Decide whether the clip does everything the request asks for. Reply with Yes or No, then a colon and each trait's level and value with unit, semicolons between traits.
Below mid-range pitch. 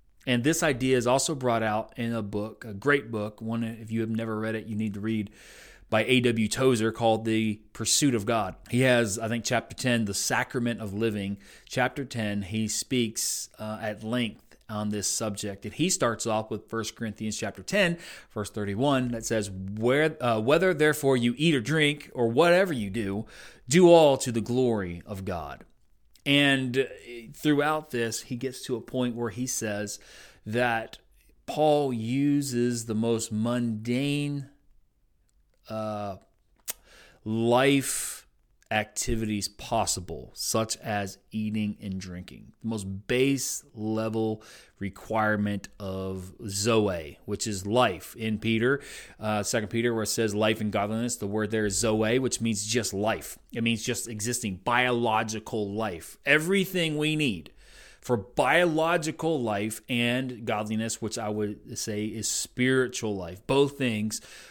Yes: low, 115 Hz